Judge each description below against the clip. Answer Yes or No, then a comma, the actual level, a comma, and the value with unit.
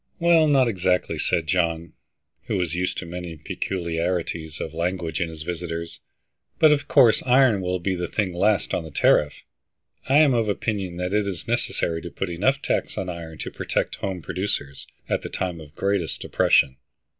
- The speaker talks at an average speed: Yes, average, 180 wpm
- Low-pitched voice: Yes, very low, 90 Hz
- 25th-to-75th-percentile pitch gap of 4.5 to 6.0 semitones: No, average, 3.7 semitones